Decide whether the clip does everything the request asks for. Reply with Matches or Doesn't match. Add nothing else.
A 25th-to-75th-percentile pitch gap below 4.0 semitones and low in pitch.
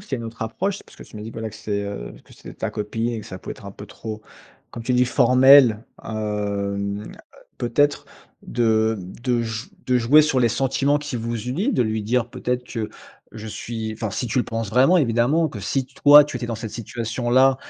Matches